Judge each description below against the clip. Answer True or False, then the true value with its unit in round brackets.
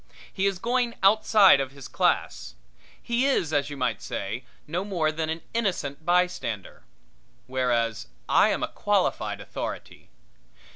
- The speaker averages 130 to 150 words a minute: True (140 wpm)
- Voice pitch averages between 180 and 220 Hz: False (160 Hz)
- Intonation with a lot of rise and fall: True (7.0 semitones)